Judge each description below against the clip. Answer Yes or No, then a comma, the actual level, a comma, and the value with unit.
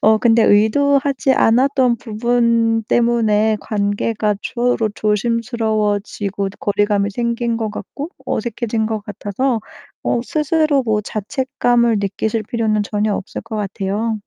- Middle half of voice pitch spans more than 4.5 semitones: No, narrow, 2.2 semitones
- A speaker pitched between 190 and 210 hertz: No, high, 225 Hz